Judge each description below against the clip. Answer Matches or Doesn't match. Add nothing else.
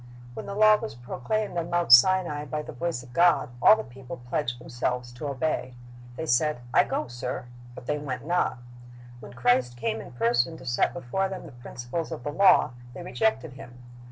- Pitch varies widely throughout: Matches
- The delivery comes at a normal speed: Matches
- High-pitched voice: Doesn't match